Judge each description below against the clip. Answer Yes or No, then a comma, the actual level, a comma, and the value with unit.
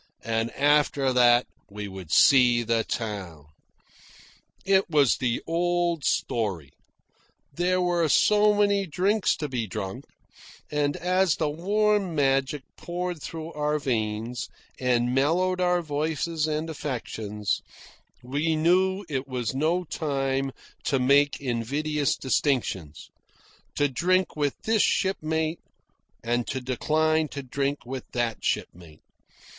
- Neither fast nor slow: No, slow, 120 wpm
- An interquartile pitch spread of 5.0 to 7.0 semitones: Yes, wide, 5.6 semitones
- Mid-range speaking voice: Yes, medium, 145 Hz